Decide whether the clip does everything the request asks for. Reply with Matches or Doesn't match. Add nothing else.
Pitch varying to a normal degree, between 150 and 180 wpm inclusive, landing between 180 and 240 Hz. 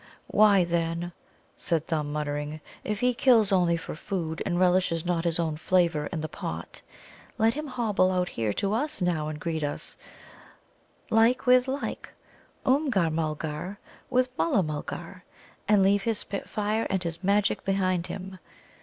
Matches